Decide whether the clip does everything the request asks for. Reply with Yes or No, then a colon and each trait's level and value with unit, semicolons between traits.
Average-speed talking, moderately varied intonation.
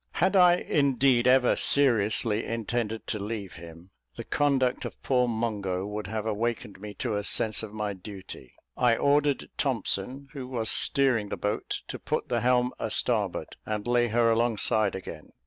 Yes: average, 165 wpm; average, 3.4 semitones